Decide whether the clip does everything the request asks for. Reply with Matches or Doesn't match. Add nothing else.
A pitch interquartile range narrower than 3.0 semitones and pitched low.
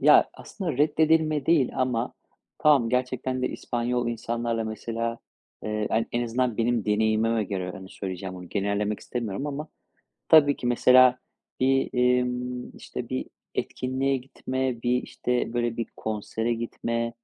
Matches